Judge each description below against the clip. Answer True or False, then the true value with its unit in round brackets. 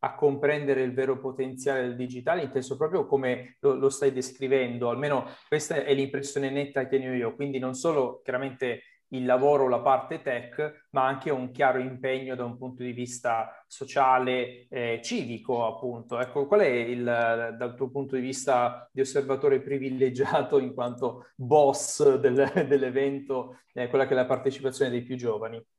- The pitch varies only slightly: True (2.0 semitones)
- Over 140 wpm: True (170 wpm)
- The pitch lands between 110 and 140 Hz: True (130 Hz)